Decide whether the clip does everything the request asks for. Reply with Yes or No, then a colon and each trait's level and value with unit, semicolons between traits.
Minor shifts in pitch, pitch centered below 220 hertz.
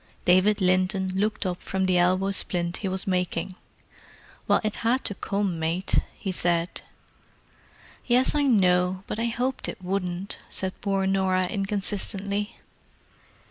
Yes: narrow, 2.1 semitones; high, 190 Hz